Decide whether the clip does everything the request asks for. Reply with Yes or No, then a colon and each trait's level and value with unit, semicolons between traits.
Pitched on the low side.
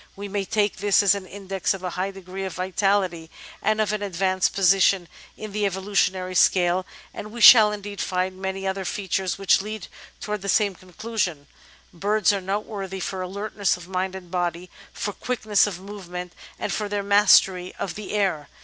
No: high, 195 Hz